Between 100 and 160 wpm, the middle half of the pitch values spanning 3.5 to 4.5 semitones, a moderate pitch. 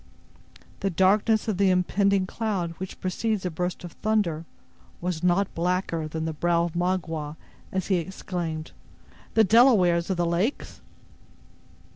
No: average, 140 wpm; narrow, 2.6 semitones; medium, 180 Hz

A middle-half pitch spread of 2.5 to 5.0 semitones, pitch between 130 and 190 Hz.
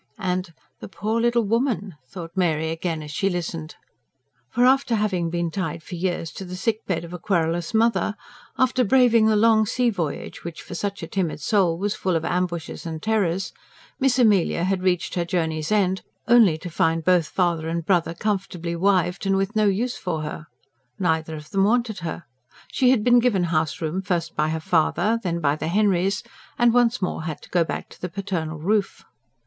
Yes: average, 4.3 semitones; medium, 185 Hz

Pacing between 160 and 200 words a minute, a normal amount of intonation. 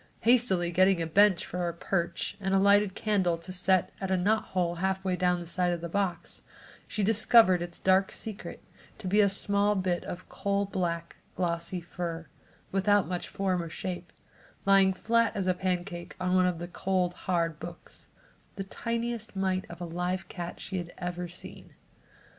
No: average, 180 wpm; narrow, 2.2 semitones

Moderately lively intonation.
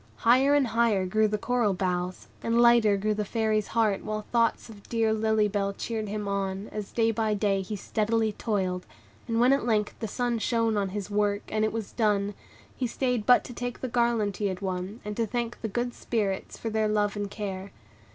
No: narrow, 2.3 semitones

